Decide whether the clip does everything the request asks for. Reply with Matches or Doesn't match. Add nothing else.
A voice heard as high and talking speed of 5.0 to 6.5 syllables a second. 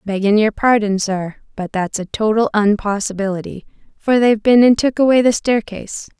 Matches